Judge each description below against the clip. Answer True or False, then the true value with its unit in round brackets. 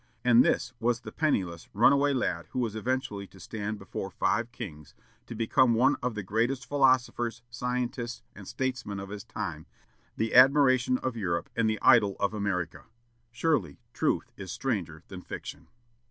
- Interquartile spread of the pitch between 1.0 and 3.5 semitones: False (4.3 semitones)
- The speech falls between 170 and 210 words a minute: False (160 wpm)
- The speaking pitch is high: False (115 Hz)